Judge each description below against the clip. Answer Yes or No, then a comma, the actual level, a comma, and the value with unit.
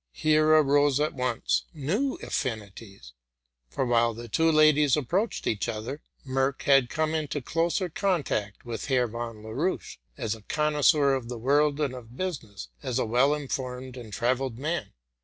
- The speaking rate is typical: Yes, average, 160 wpm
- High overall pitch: No, low, 135 Hz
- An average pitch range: Yes, average, 4.5 semitones